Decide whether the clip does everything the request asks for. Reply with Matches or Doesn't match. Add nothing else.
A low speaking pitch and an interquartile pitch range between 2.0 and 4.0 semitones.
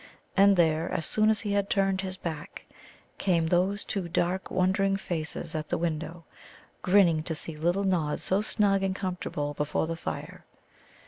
Doesn't match